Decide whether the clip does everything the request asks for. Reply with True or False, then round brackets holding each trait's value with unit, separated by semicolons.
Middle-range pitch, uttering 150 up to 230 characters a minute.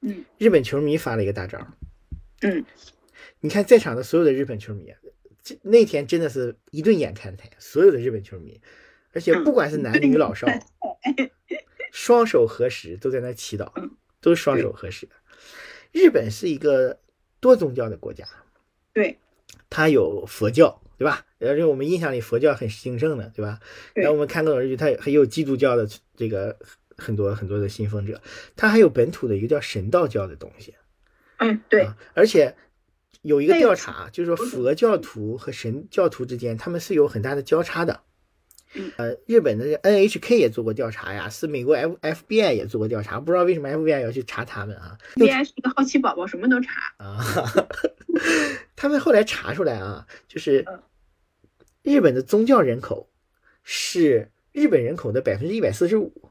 False (155 Hz; 275 characters per minute)